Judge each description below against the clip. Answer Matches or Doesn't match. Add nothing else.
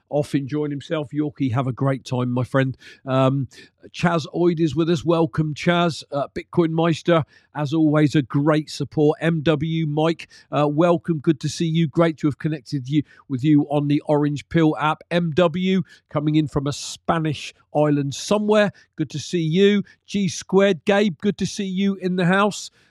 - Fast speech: Doesn't match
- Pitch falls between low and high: Matches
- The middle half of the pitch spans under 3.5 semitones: Matches